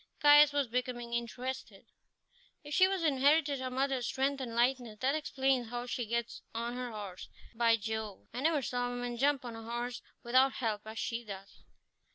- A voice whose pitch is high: Yes, high, 245 Hz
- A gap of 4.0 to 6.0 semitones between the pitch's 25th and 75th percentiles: No, narrow, 2.6 semitones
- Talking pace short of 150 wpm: No, average, 185 wpm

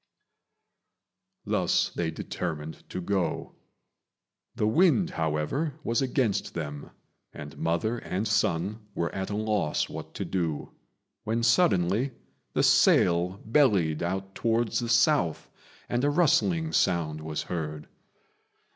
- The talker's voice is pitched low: Yes, very low, 95 Hz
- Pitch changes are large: Yes, wide, 6.3 semitones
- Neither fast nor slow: No, slow, 120 wpm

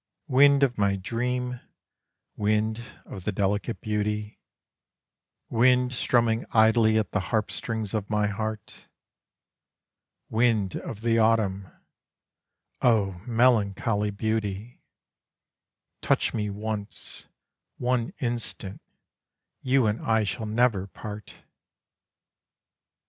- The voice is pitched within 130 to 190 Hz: No, low, 110 Hz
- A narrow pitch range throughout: Yes, narrow, 2.3 semitones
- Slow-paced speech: Yes, slow, 95 wpm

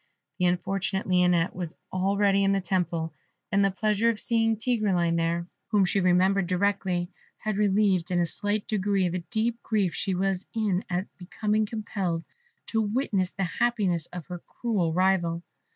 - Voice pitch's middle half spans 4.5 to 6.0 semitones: No, average, 2.8 semitones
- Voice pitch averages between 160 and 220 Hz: Yes, high, 190 Hz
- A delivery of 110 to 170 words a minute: Yes, average, 160 wpm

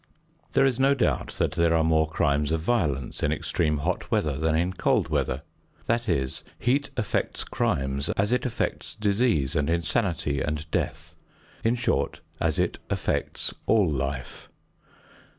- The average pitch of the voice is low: Yes, very low, 80 Hz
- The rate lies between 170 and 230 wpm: No, average, 150 wpm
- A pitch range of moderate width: No, wide, 7.7 semitones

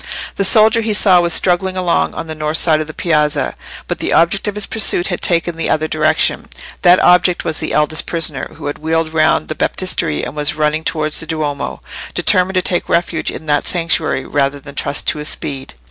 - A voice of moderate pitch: Yes, medium, 160 Hz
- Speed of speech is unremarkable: No, fast, 210 wpm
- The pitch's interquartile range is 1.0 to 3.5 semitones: Yes, average, 2.8 semitones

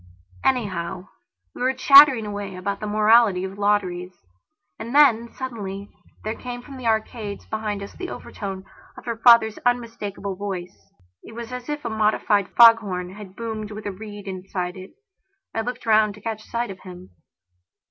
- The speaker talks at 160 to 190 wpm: Yes, average, 165 wpm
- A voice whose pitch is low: No, high, 215 Hz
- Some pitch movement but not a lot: Yes, average, 3.1 semitones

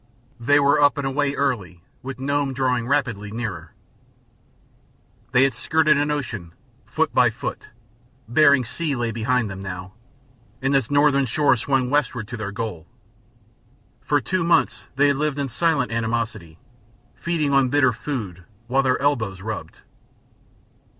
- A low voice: Yes, low, 130 Hz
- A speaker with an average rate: Yes, average, 145 wpm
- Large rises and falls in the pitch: No, average, 4.3 semitones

